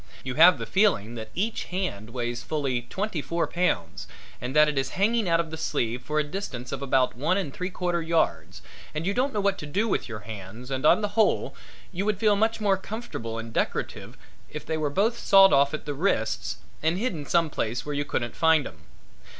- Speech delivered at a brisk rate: Yes, fast, 215 wpm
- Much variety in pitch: Yes, wide, 7.4 semitones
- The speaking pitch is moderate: Yes, medium, 155 Hz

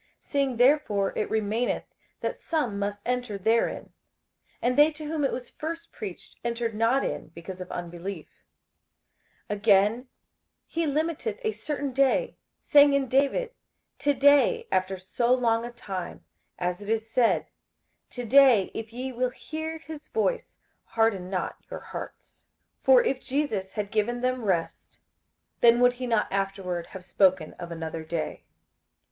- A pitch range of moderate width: No, wide, 5.8 semitones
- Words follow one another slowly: No, average, 155 wpm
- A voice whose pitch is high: Yes, high, 235 Hz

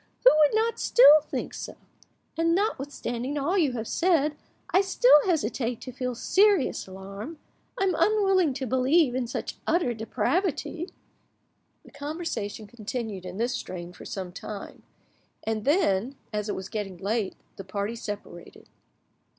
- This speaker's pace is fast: No, average, 145 wpm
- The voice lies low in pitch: No, very high, 255 Hz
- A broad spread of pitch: Yes, wide, 7.9 semitones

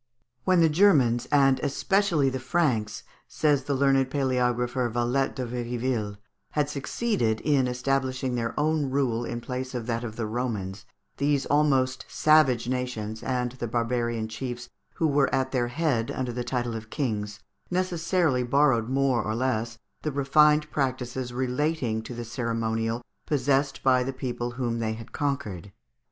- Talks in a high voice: No, low, 125 Hz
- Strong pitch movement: No, average, 3.0 semitones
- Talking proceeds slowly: No, average, 150 wpm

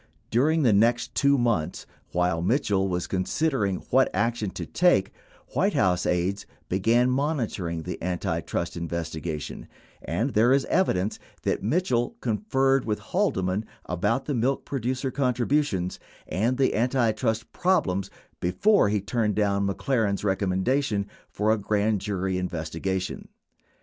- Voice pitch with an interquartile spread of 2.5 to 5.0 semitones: No, wide, 5.5 semitones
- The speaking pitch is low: Yes, low, 105 Hz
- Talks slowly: Yes, slow, 130 wpm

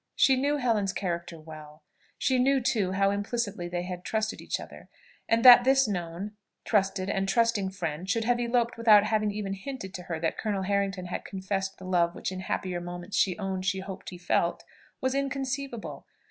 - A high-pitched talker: Yes, high, 195 Hz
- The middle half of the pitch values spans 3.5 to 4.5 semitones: Yes, average, 4.1 semitones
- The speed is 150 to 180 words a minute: No, average, 190 wpm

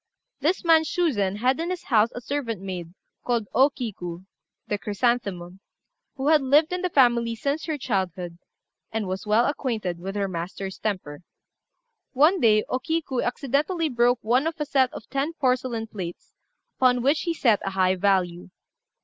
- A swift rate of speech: No, average, 165 wpm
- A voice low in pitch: No, high, 240 Hz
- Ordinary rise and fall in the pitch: No, wide, 6.5 semitones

